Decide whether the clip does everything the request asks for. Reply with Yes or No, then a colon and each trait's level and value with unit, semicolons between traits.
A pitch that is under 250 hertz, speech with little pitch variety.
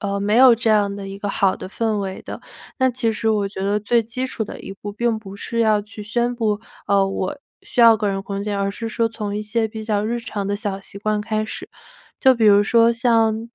Yes: high, 215 Hz; narrow, 2.2 semitones